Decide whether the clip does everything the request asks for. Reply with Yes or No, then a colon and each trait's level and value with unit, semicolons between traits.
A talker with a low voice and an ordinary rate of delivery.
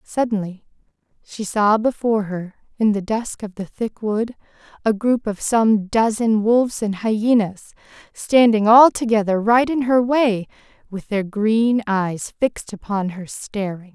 No: high, 215 Hz; average, 150 wpm